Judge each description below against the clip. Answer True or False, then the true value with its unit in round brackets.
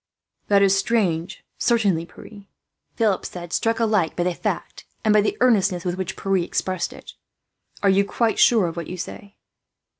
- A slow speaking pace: False (175 wpm)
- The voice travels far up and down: False (3.2 semitones)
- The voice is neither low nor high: False (195 Hz)